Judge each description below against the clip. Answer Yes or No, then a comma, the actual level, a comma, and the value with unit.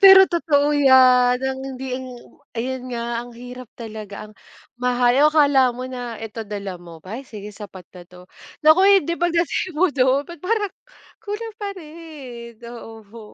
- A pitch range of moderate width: Yes, average, 4.9 semitones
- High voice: Yes, very high, 255 Hz